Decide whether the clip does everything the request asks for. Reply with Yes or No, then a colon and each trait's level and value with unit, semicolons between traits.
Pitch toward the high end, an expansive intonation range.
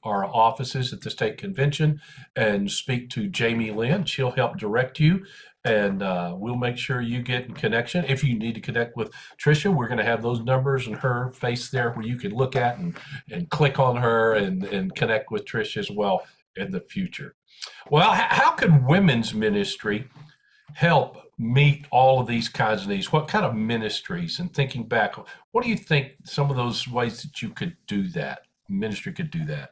No: low, 135 Hz; wide, 5.7 semitones